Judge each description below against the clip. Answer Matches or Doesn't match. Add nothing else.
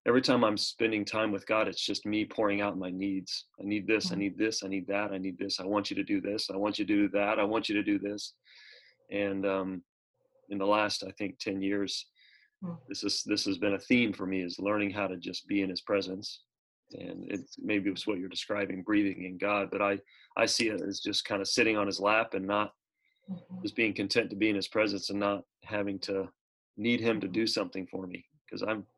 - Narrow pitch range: Matches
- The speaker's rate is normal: Doesn't match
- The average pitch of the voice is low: Matches